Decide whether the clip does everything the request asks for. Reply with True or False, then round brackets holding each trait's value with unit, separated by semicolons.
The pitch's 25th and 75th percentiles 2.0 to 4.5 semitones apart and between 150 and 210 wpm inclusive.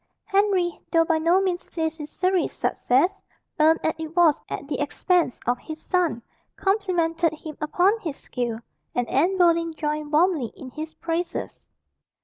True (2.9 semitones; 155 wpm)